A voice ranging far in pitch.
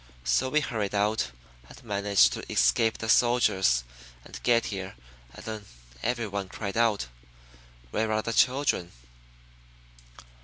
No: average, 2.8 semitones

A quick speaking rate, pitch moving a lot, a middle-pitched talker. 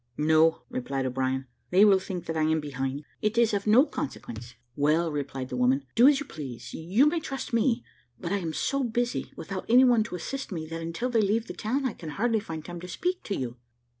Yes: fast, 225 wpm; wide, 8.0 semitones; medium, 175 Hz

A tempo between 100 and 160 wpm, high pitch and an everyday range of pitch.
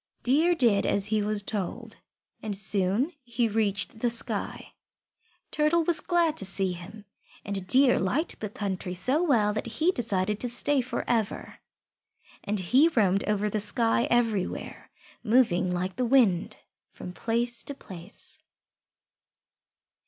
Yes: average, 140 wpm; high, 215 Hz; average, 4.3 semitones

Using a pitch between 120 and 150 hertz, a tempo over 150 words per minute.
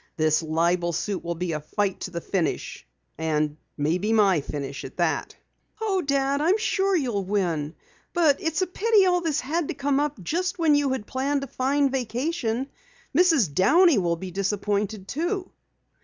No: high, 245 Hz; average, 170 wpm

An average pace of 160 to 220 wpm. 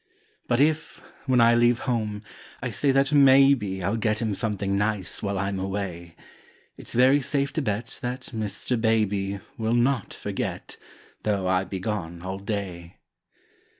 No: average, 150 wpm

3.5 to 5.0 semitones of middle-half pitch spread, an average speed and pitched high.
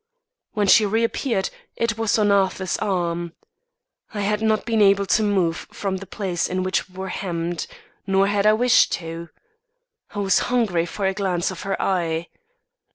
No: average, 2.9 semitones; average, 170 wpm; high, 195 Hz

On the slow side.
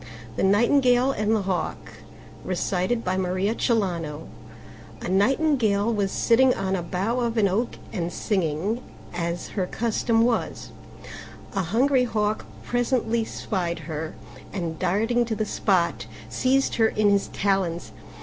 Yes: slow, 120 wpm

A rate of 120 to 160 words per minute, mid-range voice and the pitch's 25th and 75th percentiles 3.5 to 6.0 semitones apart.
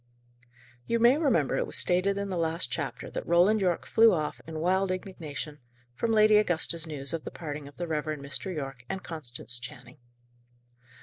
No: average, 180 wpm; medium, 165 Hz; average, 4.6 semitones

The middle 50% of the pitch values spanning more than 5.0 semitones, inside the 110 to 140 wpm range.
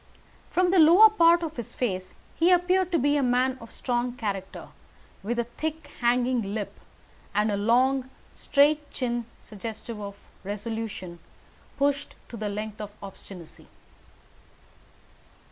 Yes: wide, 5.6 semitones; slow, 135 wpm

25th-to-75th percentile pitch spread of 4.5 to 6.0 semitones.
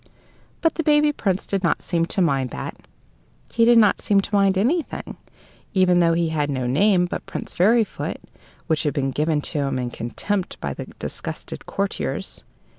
Yes: wide, 5.6 semitones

